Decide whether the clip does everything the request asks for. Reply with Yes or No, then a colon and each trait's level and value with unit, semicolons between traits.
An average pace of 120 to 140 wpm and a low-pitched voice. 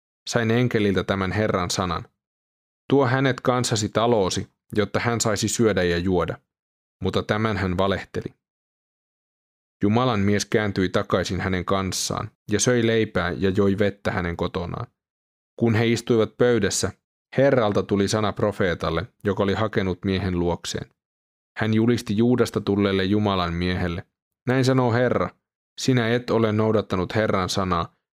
Yes: average, 130 wpm; low, 105 Hz